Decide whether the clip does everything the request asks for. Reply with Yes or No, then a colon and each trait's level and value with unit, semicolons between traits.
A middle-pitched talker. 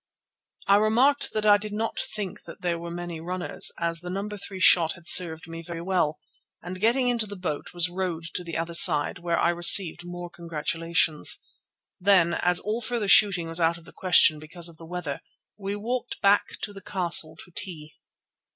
Yes: medium, 175 Hz